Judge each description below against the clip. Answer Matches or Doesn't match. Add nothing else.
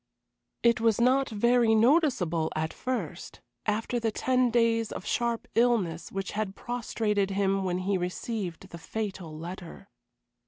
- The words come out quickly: Doesn't match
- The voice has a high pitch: Matches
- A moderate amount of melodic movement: Matches